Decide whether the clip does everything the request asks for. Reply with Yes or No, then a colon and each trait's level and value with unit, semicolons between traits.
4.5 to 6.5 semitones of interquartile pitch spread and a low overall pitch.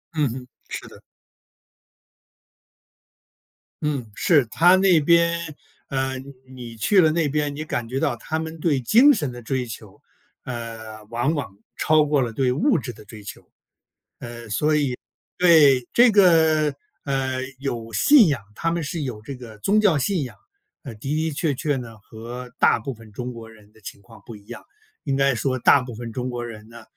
Yes: average, 5.1 semitones; low, 130 Hz